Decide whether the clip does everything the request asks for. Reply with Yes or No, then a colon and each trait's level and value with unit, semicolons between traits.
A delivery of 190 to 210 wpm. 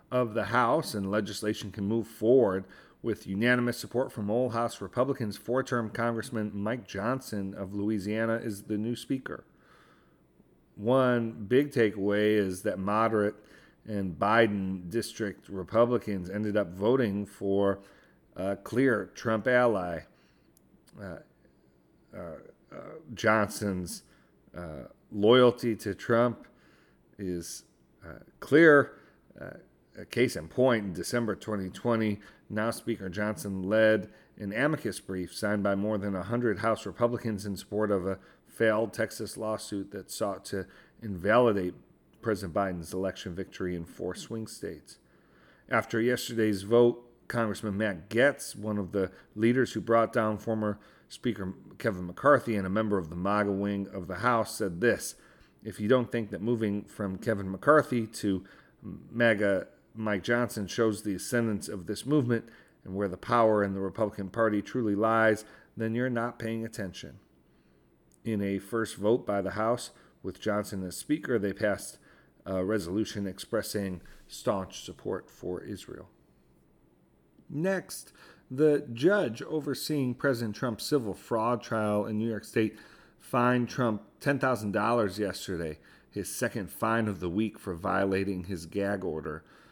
No: average, 140 wpm